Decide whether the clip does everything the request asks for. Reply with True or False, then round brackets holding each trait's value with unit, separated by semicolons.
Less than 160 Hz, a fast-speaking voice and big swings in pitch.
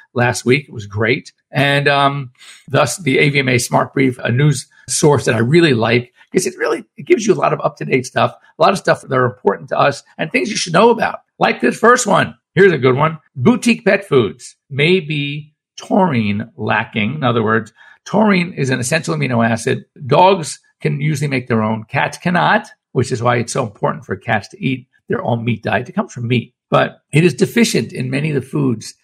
True (140 Hz; 215 wpm; 6.7 semitones)